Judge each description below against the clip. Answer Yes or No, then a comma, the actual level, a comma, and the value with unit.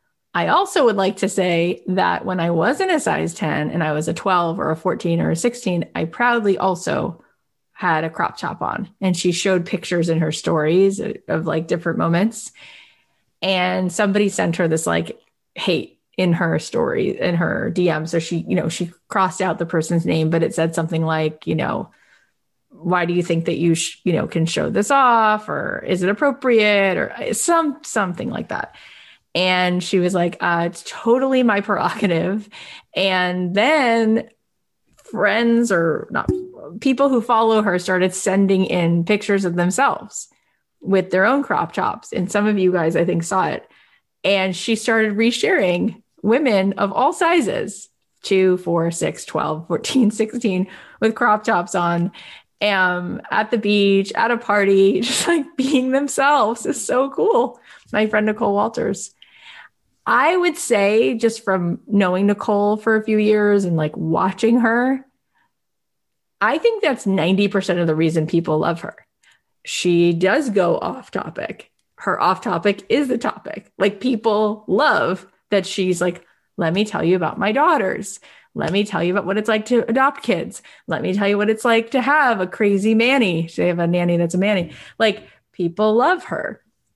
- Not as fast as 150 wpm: No, average, 175 wpm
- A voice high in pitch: Yes, high, 195 Hz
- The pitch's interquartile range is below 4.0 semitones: No, average, 4.3 semitones